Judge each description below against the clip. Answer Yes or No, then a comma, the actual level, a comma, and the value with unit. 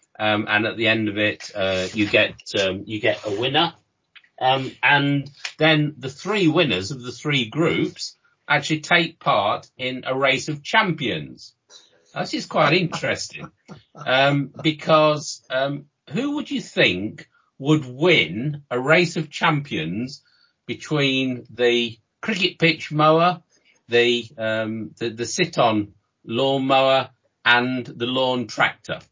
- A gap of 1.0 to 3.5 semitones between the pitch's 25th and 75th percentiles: No, average, 5.0 semitones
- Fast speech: No, slow, 135 wpm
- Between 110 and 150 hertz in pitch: Yes, low, 135 Hz